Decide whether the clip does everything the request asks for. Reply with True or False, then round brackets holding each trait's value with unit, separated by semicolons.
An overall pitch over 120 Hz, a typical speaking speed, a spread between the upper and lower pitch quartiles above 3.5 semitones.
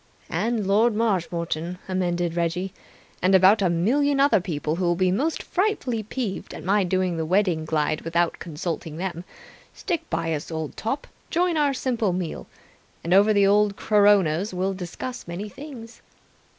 True (190 Hz; 160 wpm; 4.6 semitones)